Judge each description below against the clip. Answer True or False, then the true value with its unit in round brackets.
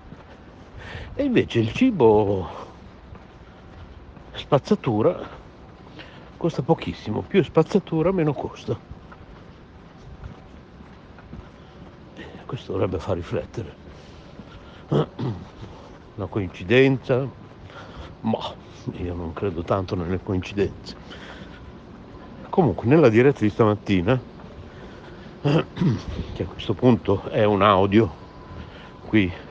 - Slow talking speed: True (75 wpm)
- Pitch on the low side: True (105 Hz)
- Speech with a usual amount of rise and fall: False (6.1 semitones)